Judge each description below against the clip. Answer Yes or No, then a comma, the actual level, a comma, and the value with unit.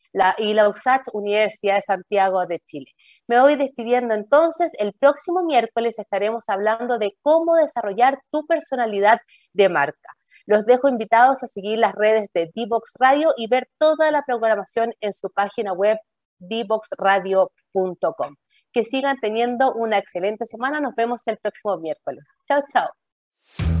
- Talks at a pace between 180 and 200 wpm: No, average, 145 wpm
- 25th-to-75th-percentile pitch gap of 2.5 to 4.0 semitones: No, average, 4.5 semitones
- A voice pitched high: Yes, high, 225 Hz